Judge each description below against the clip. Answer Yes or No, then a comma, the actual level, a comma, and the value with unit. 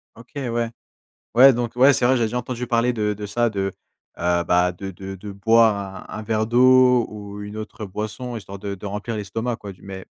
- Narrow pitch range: No, average, 3.3 semitones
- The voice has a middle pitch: No, low, 110 Hz